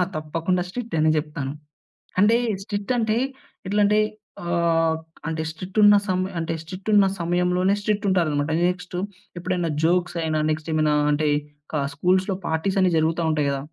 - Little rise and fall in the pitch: No, average, 3.3 semitones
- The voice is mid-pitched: Yes, medium, 175 Hz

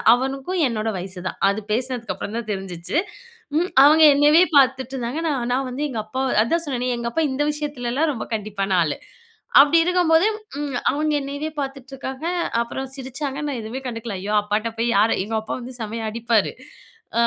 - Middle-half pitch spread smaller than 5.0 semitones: Yes, average, 4.3 semitones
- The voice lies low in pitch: No, very high, 255 Hz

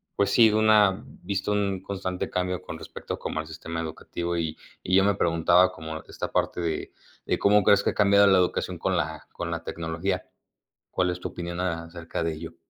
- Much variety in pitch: No, average, 2.8 semitones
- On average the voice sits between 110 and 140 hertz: No, very low, 90 Hz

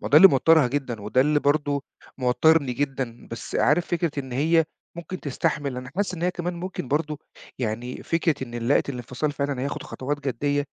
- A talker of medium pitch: Yes, medium, 145 Hz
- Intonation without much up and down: No, average, 4.0 semitones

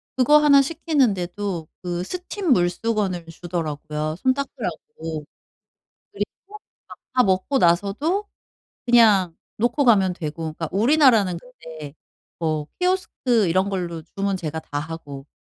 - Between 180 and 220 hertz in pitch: Yes, high, 190 Hz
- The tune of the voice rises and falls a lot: Yes, wide, 7.5 semitones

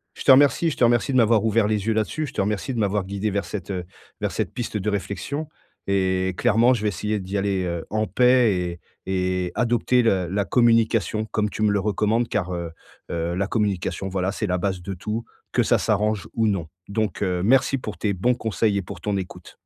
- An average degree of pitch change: Yes, average, 3.1 semitones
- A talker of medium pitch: No, low, 105 Hz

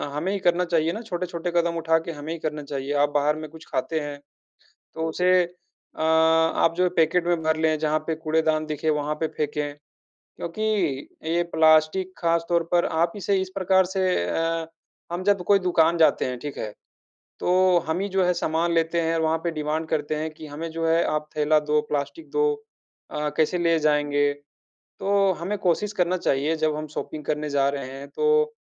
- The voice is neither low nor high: Yes, medium, 160 Hz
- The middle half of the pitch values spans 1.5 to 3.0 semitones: Yes, narrow, 2.4 semitones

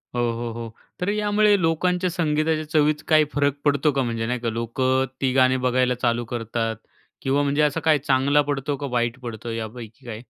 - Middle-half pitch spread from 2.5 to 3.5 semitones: No, average, 4.3 semitones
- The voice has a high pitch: No, low, 135 Hz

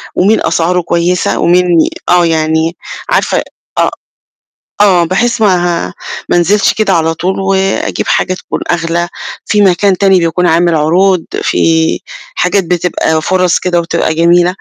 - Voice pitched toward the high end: No, medium, 175 Hz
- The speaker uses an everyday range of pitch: No, narrow, 2.2 semitones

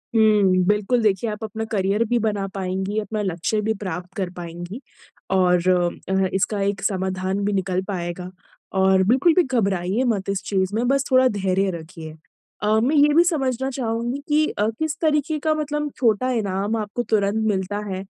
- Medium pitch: No, high, 205 Hz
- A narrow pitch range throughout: No, average, 4.2 semitones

